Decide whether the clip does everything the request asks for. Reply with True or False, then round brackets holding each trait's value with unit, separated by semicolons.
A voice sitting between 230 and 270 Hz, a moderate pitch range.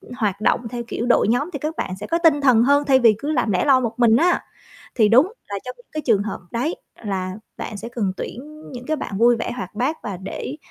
True (240 Hz; 4.7 semitones)